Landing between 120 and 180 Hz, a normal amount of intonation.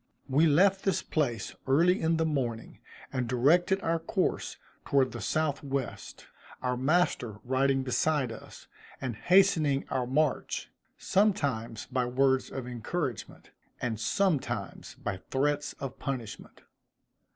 Yes: low, 135 Hz; average, 4.2 semitones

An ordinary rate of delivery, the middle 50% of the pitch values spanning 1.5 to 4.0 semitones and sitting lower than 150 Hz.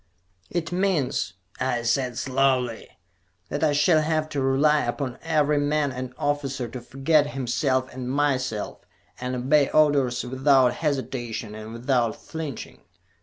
No: slow, 130 wpm; average, 2.9 semitones; low, 135 Hz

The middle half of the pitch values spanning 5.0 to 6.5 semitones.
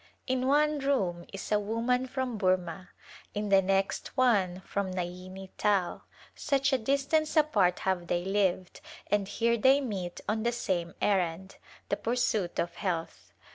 Yes: average, 5.3 semitones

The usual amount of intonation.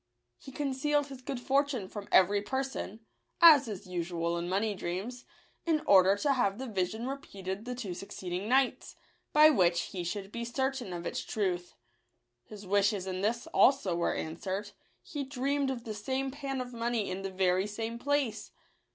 No: wide, 5.9 semitones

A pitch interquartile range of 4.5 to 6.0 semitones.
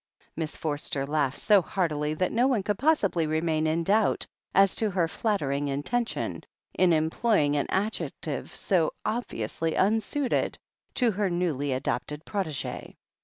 Yes: wide, 5.6 semitones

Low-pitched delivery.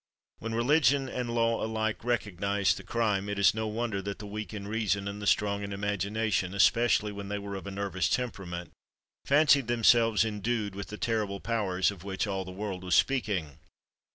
Yes: low, 105 Hz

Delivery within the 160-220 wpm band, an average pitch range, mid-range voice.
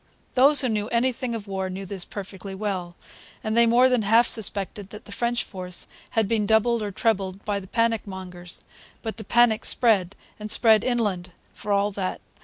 No: average, 190 wpm; average, 3.2 semitones; high, 210 Hz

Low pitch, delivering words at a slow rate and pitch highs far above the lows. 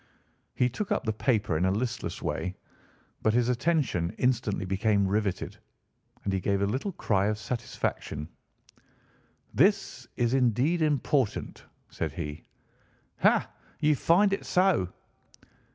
Yes: low, 120 Hz; slow, 130 wpm; wide, 6.0 semitones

